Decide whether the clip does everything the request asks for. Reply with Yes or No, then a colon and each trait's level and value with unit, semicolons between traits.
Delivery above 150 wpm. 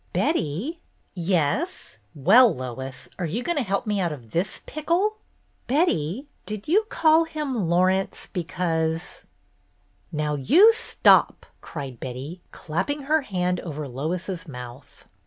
No: average, 145 wpm